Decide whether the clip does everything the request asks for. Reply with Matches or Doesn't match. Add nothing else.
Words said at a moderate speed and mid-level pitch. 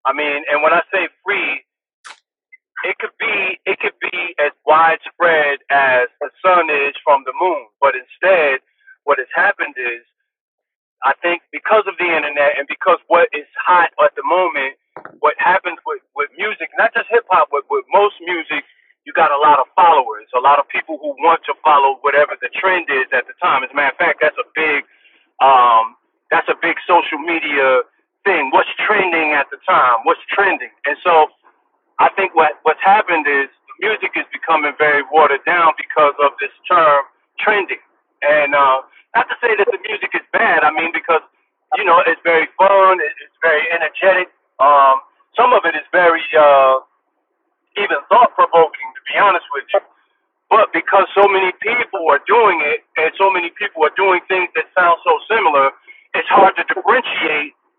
Matches